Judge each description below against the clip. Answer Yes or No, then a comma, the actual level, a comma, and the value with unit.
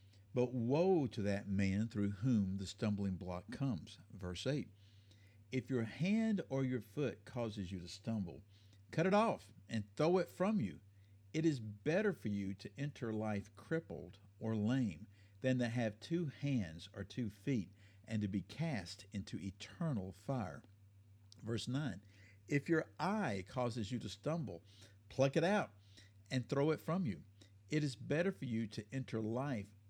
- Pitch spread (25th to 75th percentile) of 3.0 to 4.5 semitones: No, average, 5.1 semitones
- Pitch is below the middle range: Yes, low, 110 Hz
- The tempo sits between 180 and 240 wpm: No, average, 165 wpm